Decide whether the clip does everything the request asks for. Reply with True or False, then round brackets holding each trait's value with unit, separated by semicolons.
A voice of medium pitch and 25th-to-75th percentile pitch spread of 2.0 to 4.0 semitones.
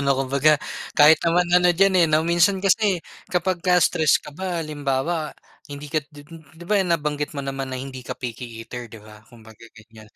False (150 Hz; 4.7 semitones)